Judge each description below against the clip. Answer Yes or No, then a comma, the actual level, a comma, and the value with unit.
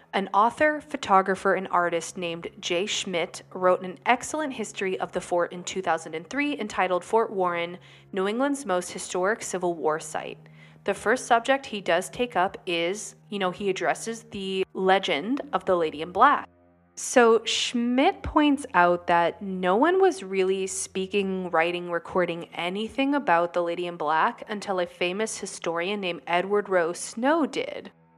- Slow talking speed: No, average, 155 wpm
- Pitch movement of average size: Yes, average, 4.0 semitones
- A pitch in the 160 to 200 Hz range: Yes, high, 190 Hz